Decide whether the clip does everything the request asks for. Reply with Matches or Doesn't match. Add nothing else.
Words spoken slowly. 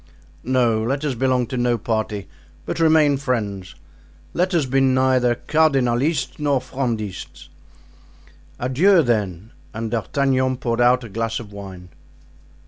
Matches